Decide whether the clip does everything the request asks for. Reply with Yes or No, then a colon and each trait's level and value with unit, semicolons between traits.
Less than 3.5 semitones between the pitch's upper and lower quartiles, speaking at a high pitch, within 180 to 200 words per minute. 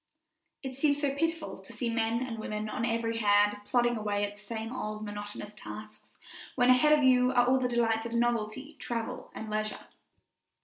Yes: average, 2.9 semitones; high, 230 Hz; average, 185 wpm